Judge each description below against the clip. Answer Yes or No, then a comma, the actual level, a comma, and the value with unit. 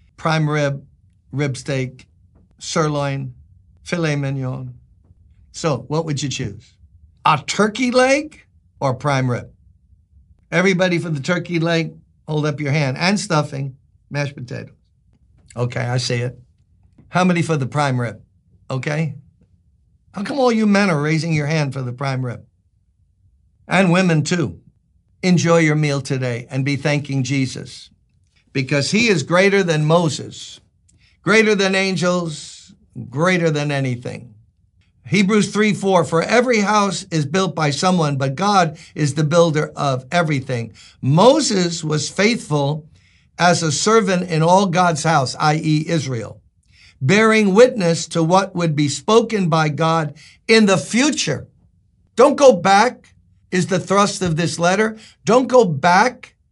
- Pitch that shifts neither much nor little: No, wide, 6.6 semitones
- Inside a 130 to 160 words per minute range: Yes, average, 140 wpm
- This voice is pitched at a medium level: Yes, medium, 150 Hz